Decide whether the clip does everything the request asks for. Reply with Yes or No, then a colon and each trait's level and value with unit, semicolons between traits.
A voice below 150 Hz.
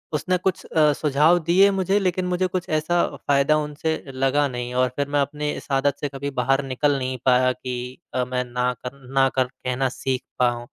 Yes: medium, 140 Hz